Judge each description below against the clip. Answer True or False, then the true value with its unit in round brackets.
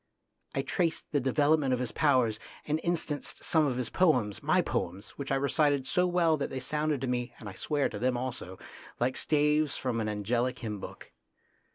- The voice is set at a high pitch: False (135 Hz)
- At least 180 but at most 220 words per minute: True (195 wpm)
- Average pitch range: True (3.9 semitones)